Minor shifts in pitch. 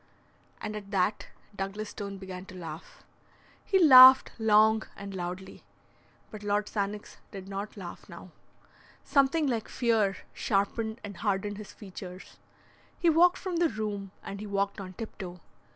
Yes: narrow, 2.3 semitones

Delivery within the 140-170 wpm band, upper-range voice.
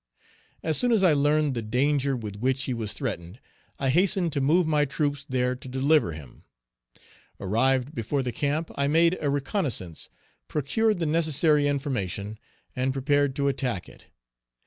No: average, 160 wpm; medium, 140 Hz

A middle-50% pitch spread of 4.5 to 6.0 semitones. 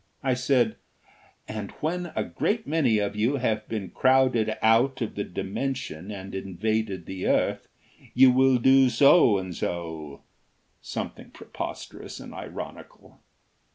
Yes: average, 5.1 semitones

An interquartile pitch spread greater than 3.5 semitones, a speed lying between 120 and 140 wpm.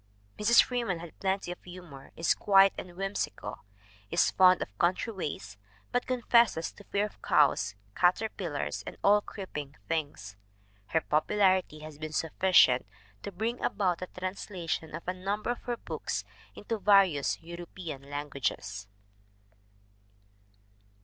Yes: average, 4.7 semitones; slow, 135 wpm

